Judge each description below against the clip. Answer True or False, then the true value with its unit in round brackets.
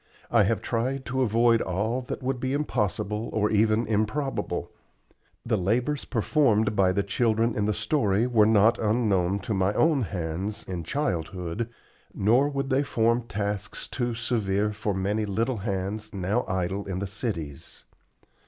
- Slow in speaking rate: False (155 wpm)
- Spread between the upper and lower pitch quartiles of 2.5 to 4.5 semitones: True (3.3 semitones)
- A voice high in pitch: False (110 Hz)